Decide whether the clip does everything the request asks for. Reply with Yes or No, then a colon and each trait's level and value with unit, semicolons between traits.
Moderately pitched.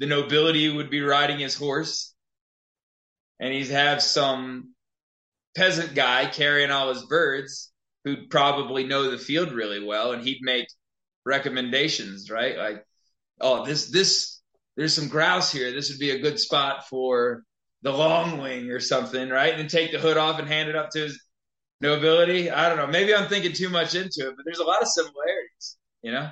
Yes: medium, 145 Hz